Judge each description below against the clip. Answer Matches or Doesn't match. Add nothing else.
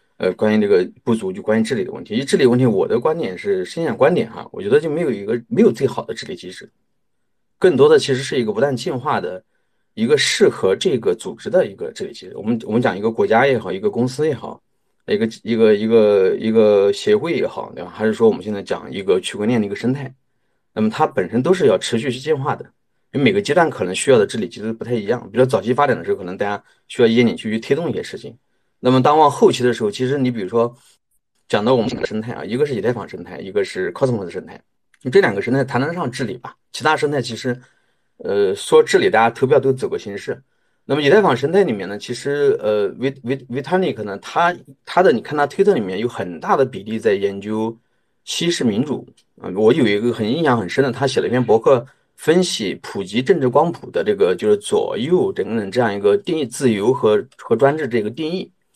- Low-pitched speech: Doesn't match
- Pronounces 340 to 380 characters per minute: Matches